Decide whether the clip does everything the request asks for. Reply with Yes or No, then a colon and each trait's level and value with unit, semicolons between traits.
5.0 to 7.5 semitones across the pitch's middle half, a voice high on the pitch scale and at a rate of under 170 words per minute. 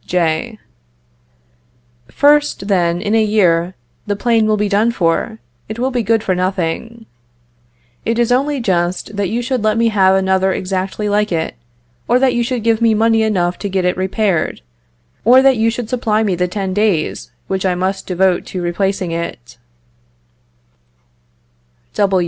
No: average, 3.7 semitones; high, 205 Hz; average, 160 wpm